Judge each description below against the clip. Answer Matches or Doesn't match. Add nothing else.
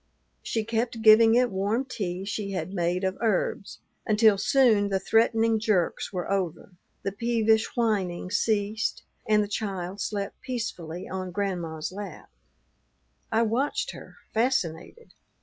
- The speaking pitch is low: Doesn't match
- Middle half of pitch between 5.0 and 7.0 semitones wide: Doesn't match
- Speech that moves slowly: Matches